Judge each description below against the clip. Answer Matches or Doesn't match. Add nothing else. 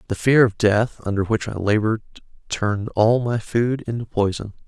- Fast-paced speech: Doesn't match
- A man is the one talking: Matches